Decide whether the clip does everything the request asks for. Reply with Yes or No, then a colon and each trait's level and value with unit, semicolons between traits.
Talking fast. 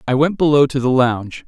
Yes: fast, 245 wpm